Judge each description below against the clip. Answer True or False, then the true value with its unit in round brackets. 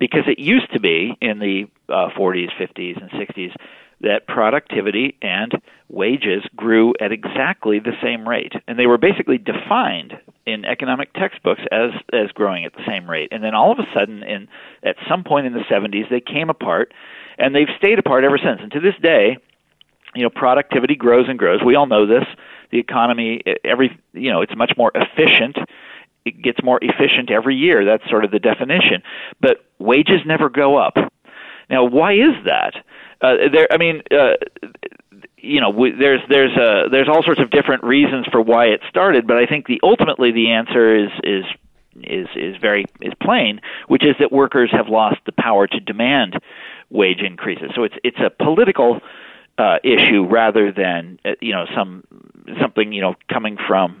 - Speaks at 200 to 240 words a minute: False (185 wpm)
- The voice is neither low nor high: False (125 Hz)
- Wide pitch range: True (6.4 semitones)